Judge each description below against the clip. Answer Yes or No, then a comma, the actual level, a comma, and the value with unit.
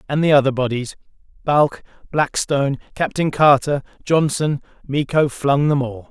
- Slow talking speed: Yes, slow, 120 wpm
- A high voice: No, medium, 140 Hz